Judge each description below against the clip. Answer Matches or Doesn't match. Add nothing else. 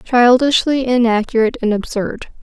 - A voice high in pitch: Matches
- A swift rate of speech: Doesn't match